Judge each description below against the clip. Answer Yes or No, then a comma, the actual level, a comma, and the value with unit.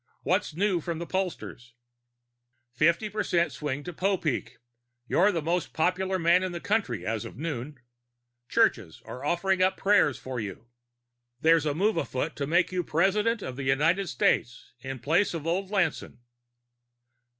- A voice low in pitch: No, medium, 165 Hz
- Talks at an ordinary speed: Yes, average, 155 wpm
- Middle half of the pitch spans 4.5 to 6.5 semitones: Yes, average, 5.0 semitones